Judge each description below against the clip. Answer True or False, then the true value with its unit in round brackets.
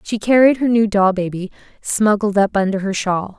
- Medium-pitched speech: False (205 Hz)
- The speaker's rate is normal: True (195 wpm)